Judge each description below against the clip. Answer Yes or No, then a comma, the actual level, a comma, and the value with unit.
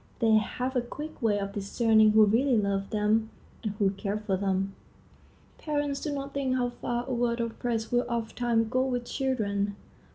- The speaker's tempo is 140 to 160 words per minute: No, average, 185 wpm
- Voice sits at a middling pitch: No, high, 230 Hz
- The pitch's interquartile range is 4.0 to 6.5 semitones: No, average, 3.2 semitones